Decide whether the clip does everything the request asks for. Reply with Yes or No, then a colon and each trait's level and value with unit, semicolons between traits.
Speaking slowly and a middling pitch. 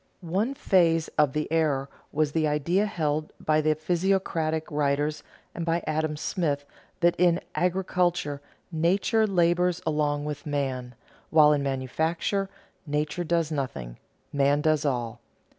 Yes: slow, 130 wpm; medium, 155 Hz